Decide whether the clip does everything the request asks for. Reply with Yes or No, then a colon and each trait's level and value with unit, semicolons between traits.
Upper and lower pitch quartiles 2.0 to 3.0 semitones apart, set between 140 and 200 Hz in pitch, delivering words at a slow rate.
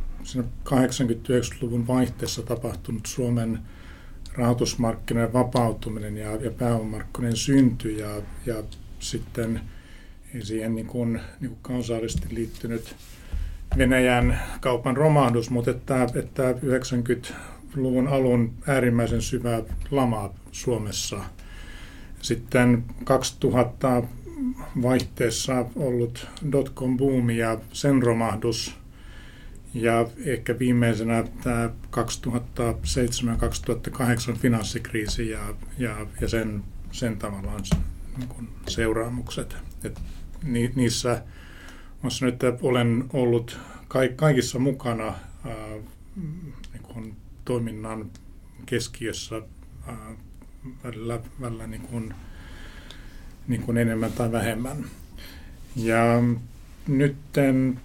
No: narrow, 2.4 semitones; low, 115 Hz; slow, 80 wpm